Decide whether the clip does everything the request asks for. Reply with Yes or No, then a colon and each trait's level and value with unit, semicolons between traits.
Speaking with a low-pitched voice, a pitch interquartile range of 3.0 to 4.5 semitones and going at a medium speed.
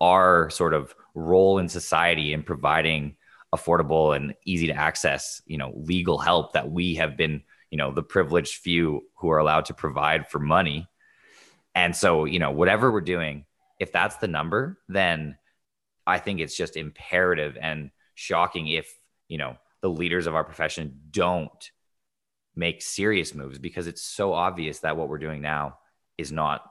No: very low, 80 Hz; narrow, 2.5 semitones; average, 170 wpm